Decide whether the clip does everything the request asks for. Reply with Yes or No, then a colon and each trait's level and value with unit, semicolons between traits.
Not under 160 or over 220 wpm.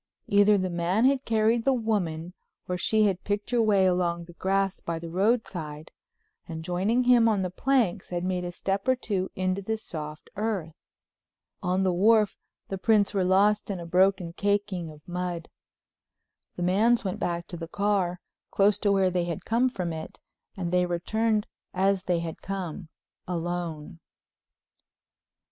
Yes: average, 165 wpm